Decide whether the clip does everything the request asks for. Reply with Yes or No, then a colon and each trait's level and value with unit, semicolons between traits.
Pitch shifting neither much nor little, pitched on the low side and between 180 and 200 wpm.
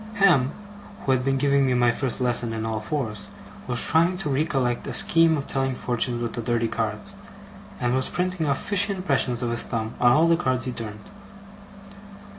Yes: average, 4.2 semitones; low, 130 Hz; average, 195 wpm